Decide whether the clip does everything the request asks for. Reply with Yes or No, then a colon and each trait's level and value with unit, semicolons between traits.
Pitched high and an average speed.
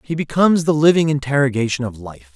No: medium, 140 Hz; average, 180 wpm